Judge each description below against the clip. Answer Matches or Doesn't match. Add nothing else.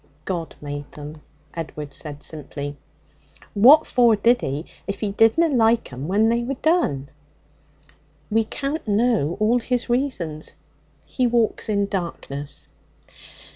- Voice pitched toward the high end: Matches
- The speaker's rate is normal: Doesn't match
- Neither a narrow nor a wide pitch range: Doesn't match